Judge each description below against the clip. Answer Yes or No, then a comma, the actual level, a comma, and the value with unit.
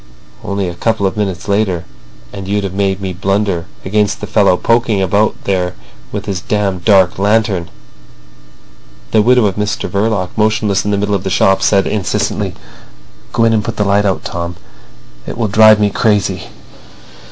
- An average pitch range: No, narrow, 1.9 semitones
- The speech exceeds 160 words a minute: Yes, average, 175 wpm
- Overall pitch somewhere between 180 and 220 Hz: No, low, 100 Hz